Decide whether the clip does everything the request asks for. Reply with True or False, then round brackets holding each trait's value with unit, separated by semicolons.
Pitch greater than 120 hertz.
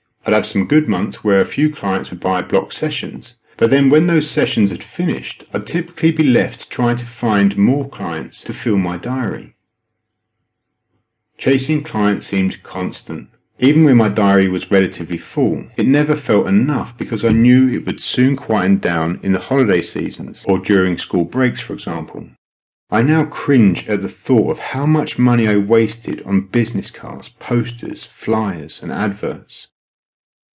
False (115 Hz)